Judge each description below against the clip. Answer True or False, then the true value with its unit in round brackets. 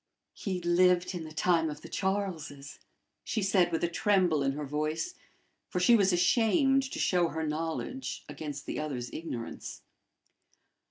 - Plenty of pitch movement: False (3.9 semitones)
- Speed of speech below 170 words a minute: True (155 wpm)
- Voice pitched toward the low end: False (170 Hz)